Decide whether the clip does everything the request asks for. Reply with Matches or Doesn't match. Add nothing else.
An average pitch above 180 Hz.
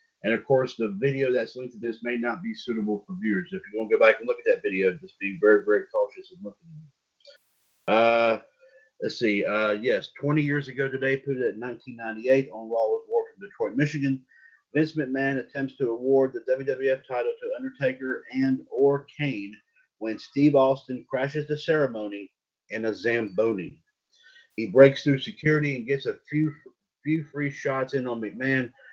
Doesn't match